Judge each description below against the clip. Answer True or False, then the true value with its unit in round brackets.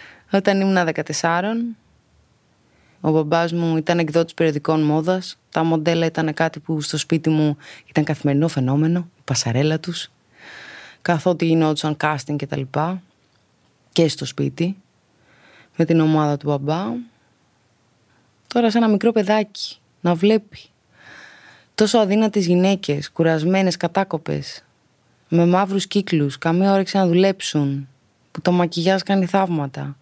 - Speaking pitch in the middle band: True (165 Hz)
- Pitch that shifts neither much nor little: True (4.0 semitones)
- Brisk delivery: False (125 wpm)